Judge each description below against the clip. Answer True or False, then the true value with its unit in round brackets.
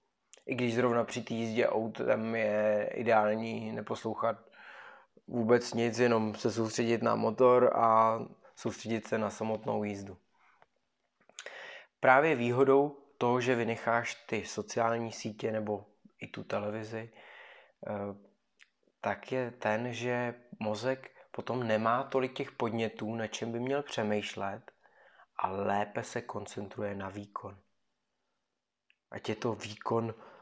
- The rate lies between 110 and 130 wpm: True (120 wpm)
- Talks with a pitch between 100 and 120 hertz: True (115 Hz)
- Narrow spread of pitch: True (2.1 semitones)